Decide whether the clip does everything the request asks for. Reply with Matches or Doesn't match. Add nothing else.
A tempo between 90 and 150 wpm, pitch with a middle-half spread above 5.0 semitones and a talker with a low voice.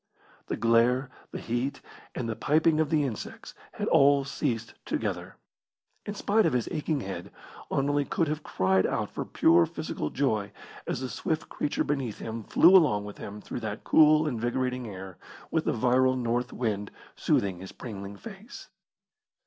Doesn't match